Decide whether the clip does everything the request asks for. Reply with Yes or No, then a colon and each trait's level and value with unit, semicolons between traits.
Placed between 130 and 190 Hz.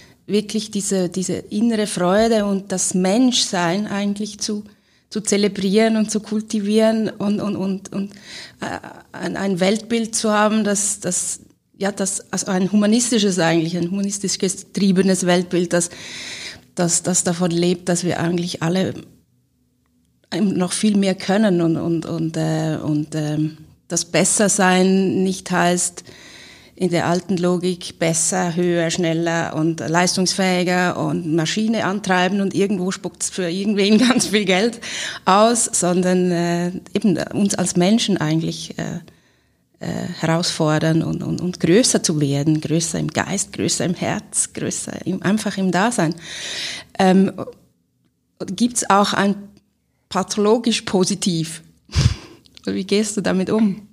Yes: medium, 185 Hz